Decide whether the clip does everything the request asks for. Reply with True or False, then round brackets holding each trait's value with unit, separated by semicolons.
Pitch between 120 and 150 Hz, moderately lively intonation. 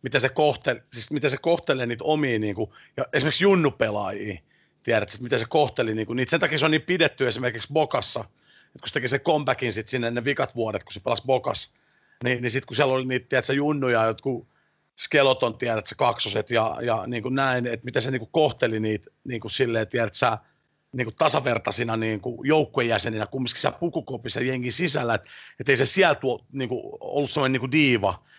True (130 Hz; 3.6 semitones)